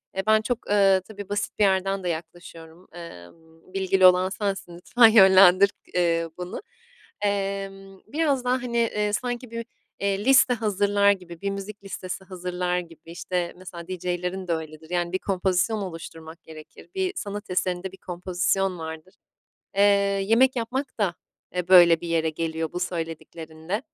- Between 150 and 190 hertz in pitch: Yes, medium, 185 Hz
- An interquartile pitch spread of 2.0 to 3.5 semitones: Yes, average, 2.9 semitones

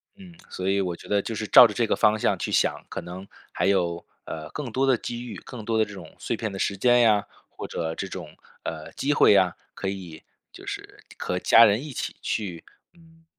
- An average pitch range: Yes, average, 4.4 semitones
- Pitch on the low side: Yes, low, 105 Hz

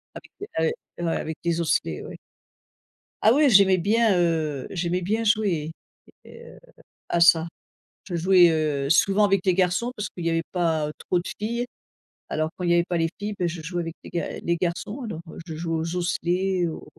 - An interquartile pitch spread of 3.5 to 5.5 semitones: No, average, 2.9 semitones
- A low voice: No, medium, 175 Hz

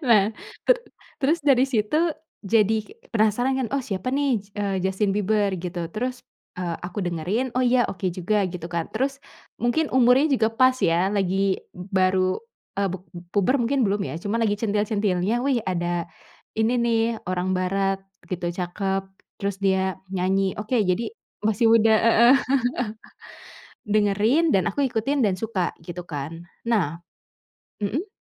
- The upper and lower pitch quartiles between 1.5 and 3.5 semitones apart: No, average, 4.2 semitones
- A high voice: Yes, high, 205 Hz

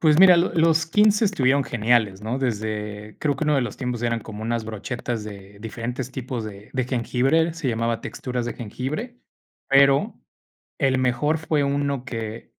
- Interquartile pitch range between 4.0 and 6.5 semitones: Yes, average, 4.5 semitones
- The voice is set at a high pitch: No, low, 125 Hz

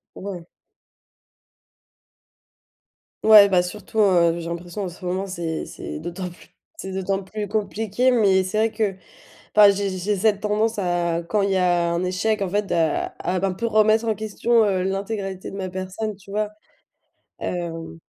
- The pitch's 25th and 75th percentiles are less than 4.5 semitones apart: Yes, average, 2.9 semitones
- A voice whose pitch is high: Yes, high, 195 Hz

